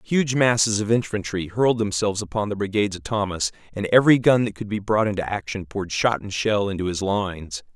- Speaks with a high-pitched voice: No, low, 105 Hz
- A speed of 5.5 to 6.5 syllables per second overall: Yes, 6.0 syllables/s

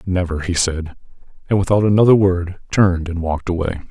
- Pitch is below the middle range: Yes, very low, 90 Hz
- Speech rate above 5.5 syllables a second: Yes, 5.9 syllables/s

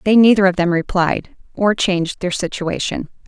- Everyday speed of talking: Yes, average, 165 wpm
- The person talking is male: No, female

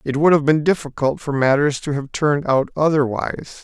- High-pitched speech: No, medium, 145 Hz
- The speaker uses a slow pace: No, average, 200 wpm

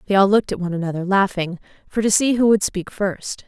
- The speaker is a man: No, female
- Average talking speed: No, fast, 240 wpm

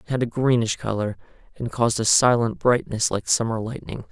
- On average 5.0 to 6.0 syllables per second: Yes, 5.6 syllables/s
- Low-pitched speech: Yes, low, 115 Hz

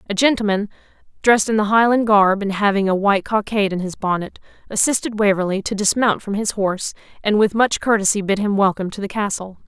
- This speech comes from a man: No, female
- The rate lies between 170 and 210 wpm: Yes, average, 200 wpm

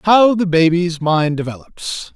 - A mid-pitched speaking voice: Yes, medium, 175 Hz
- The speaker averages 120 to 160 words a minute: Yes, average, 140 wpm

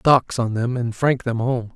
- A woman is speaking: No, male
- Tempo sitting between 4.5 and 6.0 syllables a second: No, 4.1 syllables/s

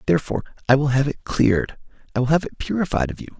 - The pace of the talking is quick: Yes, fast, 230 wpm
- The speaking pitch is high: No, low, 135 Hz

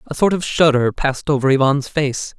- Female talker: No, male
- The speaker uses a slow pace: No, average, 200 wpm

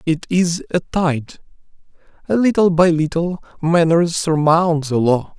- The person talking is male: Yes, male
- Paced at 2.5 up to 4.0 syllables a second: Yes, 3.7 syllables/s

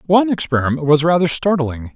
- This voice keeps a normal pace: Yes, average, 155 wpm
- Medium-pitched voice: Yes, medium, 160 Hz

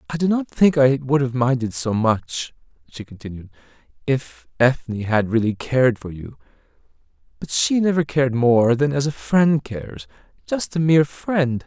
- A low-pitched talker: Yes, low, 130 Hz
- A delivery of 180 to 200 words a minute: No, average, 170 wpm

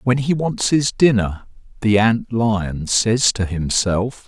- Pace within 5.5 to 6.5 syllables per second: No, 3.4 syllables/s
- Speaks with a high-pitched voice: No, low, 110 Hz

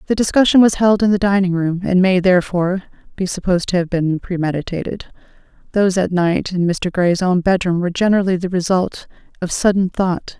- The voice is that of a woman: Yes, female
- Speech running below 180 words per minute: No, average, 185 wpm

